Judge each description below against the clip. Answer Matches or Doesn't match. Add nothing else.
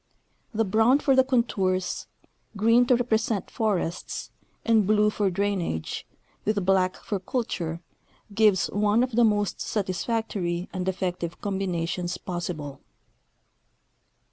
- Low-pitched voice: Doesn't match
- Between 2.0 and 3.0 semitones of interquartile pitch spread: Doesn't match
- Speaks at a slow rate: Matches